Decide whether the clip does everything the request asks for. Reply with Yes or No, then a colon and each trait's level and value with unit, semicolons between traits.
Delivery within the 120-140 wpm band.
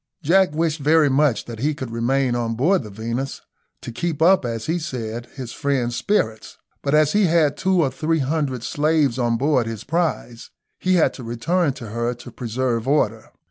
No: average, 190 wpm